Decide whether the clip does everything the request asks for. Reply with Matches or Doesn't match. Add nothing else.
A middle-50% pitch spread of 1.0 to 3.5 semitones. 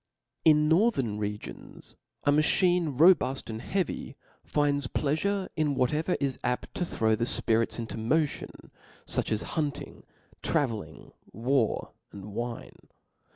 Doesn't match